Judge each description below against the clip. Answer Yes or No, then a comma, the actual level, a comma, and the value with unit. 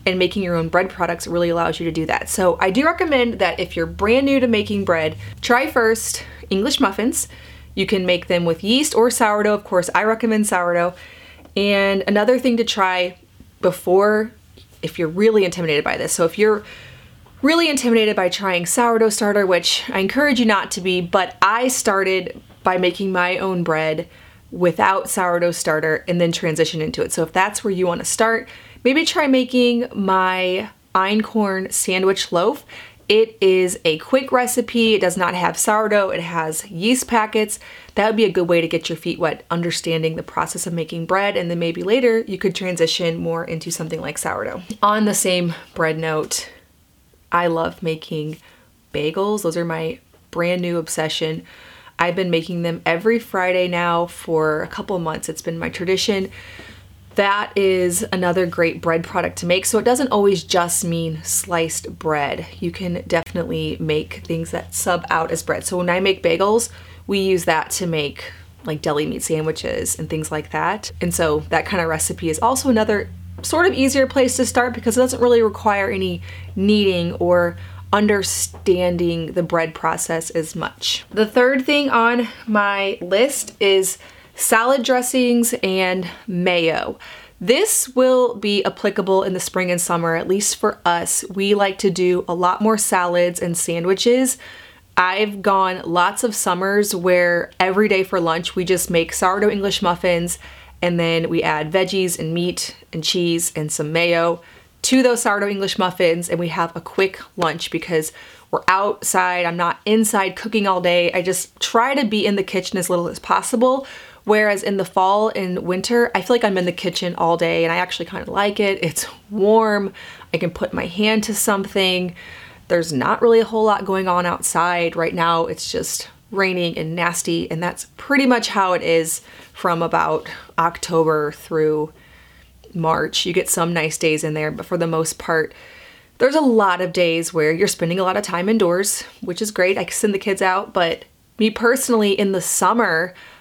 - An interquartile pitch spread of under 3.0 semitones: No, average, 4.0 semitones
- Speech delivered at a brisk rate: No, average, 185 wpm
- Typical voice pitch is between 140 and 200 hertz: Yes, medium, 185 Hz